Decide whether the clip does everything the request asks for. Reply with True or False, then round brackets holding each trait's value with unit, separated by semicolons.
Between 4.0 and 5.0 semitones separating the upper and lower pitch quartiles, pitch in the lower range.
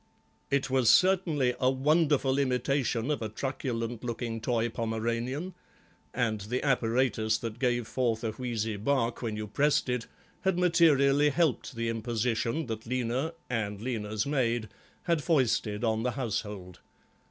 False (3.5 semitones; 120 Hz)